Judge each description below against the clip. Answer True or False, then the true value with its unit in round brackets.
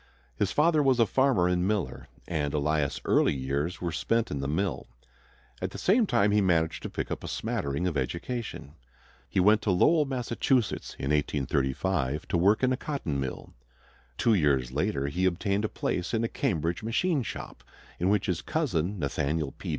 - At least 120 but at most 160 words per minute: False (180 wpm)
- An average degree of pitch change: False (7.5 semitones)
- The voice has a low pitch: True (90 Hz)